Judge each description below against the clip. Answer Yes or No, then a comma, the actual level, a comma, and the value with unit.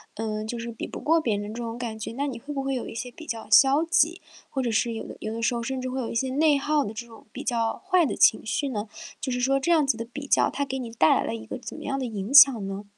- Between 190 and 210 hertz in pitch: No, high, 245 Hz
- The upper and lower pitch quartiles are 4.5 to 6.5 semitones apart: No, average, 3.5 semitones